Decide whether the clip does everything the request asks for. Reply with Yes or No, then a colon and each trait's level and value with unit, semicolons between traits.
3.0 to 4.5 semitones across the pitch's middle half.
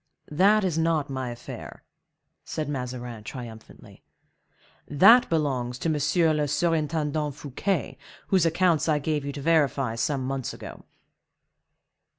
Yes: average, 3.8 semitones